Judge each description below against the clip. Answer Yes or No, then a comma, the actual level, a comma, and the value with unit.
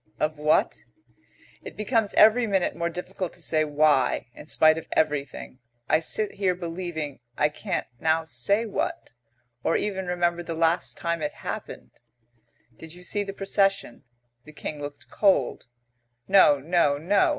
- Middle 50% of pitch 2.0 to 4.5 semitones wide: Yes, average, 4.1 semitones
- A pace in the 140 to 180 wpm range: Yes, average, 150 wpm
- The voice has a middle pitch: Yes, medium, 170 Hz